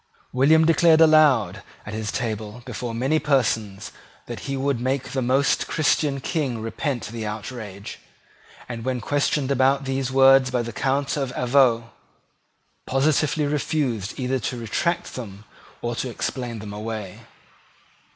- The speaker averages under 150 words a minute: Yes, average, 140 wpm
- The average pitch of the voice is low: Yes, low, 130 Hz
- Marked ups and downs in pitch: No, average, 3.6 semitones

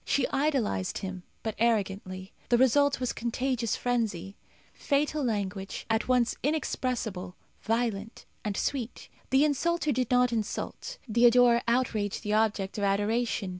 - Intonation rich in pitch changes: No, average, 3.8 semitones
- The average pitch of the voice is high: Yes, high, 235 Hz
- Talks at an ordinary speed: No, slow, 130 wpm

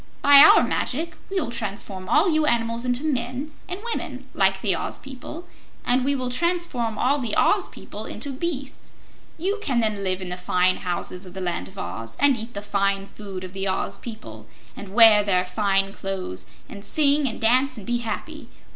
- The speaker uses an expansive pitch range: Yes, wide, 6.0 semitones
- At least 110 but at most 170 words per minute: No, average, 195 wpm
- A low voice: No, high, 230 Hz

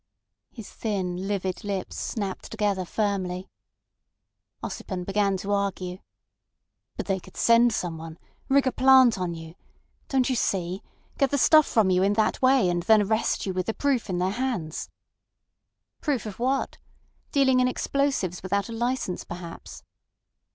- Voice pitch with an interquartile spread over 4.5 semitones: Yes, average, 5.1 semitones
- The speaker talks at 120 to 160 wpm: Yes, average, 150 wpm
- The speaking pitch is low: No, high, 200 Hz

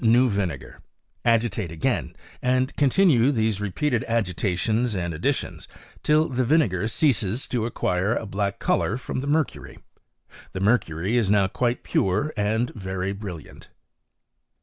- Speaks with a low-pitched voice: Yes, low, 110 Hz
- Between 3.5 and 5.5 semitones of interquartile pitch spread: Yes, average, 4.7 semitones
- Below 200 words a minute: Yes, average, 140 wpm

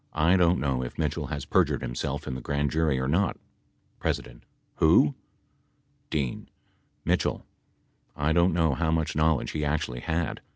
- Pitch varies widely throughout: No, average, 2.7 semitones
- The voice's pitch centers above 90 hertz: No, very low, 75 Hz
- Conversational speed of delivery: Yes, average, 155 wpm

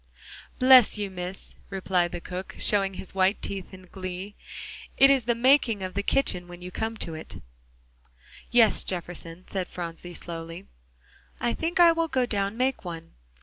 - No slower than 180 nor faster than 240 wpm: No, average, 160 wpm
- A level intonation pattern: No, average, 4.8 semitones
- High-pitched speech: Yes, high, 195 Hz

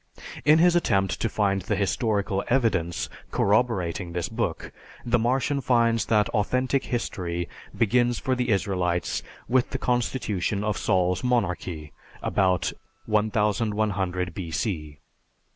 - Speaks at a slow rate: Yes, slow, 115 wpm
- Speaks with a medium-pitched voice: No, low, 105 Hz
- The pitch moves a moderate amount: Yes, average, 4.7 semitones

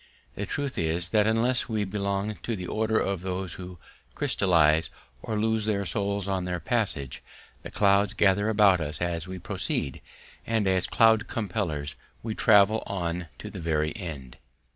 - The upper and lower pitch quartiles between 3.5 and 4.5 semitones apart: Yes, average, 3.8 semitones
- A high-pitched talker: No, low, 100 Hz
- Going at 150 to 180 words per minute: Yes, average, 165 wpm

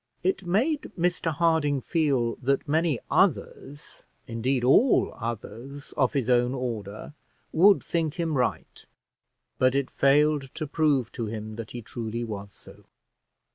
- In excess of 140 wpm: No, slow, 135 wpm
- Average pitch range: Yes, average, 5.0 semitones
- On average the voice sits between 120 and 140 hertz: Yes, low, 135 Hz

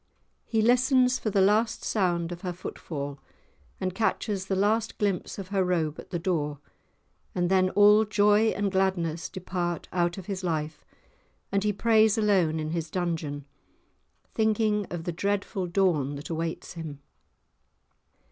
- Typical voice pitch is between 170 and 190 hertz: Yes, medium, 185 Hz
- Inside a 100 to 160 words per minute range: Yes, average, 150 wpm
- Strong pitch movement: No, average, 3.8 semitones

